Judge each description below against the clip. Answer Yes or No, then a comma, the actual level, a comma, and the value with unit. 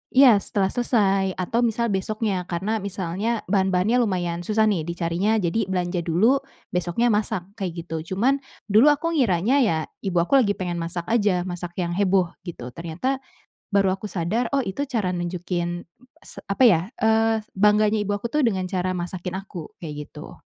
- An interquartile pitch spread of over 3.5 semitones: Yes, average, 4.0 semitones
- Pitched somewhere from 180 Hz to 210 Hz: Yes, high, 190 Hz